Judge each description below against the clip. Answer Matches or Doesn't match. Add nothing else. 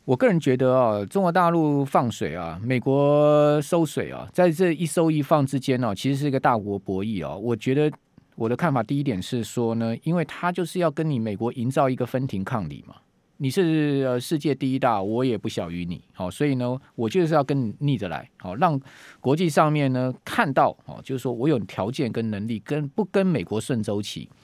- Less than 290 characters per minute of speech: Doesn't match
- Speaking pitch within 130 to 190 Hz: Matches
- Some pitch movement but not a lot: Matches